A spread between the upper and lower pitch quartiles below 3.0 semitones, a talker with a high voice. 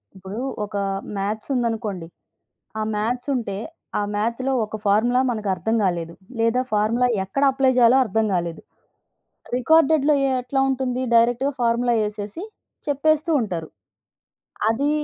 No: average, 3.8 semitones; high, 230 Hz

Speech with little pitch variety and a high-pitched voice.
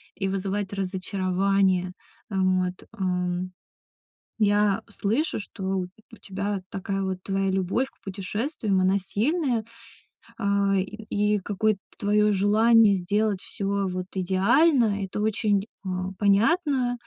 Yes: narrow, 2.0 semitones; high, 200 Hz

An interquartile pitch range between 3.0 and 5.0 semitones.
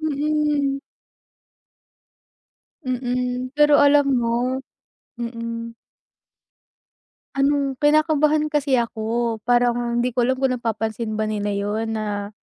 Yes: average, 3.6 semitones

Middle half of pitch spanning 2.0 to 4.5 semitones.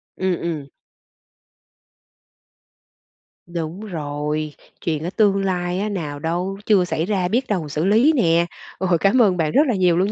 Yes: average, 3.4 semitones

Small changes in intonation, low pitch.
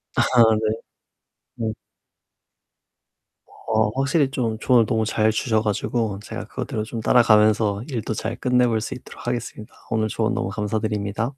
Yes: narrow, 1.8 semitones; low, 110 Hz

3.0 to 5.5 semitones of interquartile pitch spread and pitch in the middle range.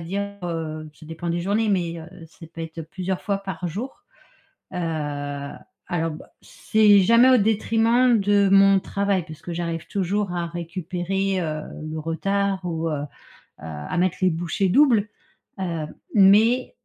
Yes: average, 3.5 semitones; medium, 180 Hz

